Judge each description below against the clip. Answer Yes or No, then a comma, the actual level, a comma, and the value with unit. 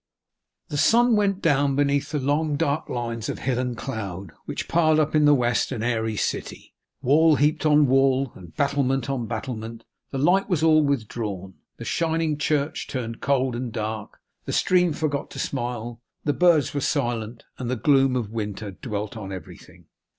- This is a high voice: No, low, 135 Hz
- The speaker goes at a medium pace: Yes, average, 175 wpm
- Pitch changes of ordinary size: Yes, average, 4.5 semitones